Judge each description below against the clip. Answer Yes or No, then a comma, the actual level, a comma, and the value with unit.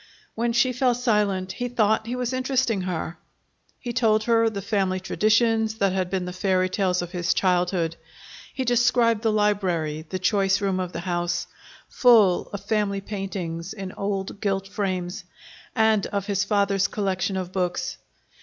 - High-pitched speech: Yes, high, 200 Hz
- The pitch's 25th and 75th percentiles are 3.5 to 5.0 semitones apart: No, average, 3.1 semitones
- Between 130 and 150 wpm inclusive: No, average, 165 wpm